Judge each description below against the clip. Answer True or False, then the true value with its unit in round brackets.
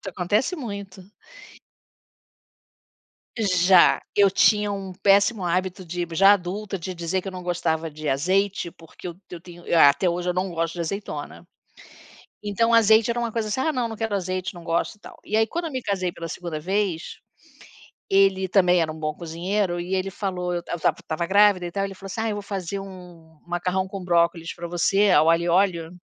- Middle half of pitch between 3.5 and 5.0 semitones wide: False (2.8 semitones)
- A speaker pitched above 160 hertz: True (185 Hz)